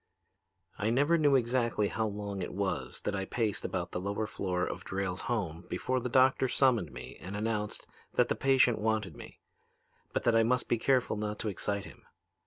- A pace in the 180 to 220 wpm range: Yes, average, 190 wpm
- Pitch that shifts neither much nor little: Yes, average, 3.8 semitones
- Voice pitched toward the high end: No, low, 110 Hz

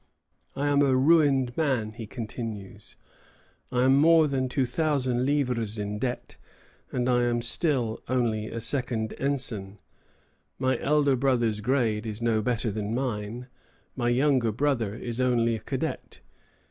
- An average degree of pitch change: Yes, average, 3.2 semitones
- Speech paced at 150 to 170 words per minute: No, average, 140 wpm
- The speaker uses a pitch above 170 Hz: No, low, 125 Hz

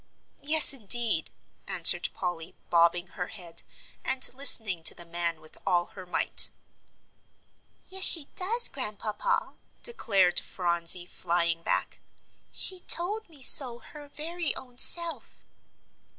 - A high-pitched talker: Yes, high, 215 Hz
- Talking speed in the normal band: No, slow, 120 wpm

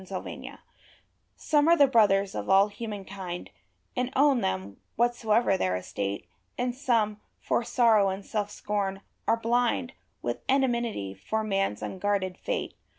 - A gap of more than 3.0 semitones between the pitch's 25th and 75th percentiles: Yes, average, 3.8 semitones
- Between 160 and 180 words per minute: No, average, 140 wpm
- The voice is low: No, high, 210 Hz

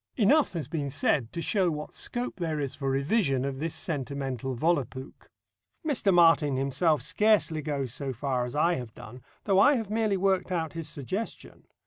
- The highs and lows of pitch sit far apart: Yes, wide, 5.8 semitones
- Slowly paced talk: No, average, 175 wpm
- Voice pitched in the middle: Yes, medium, 155 Hz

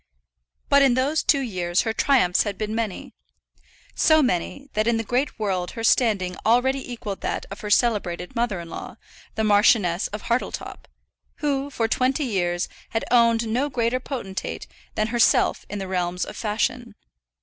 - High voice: Yes, high, 225 Hz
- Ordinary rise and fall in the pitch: Yes, average, 4.3 semitones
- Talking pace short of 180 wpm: Yes, average, 165 wpm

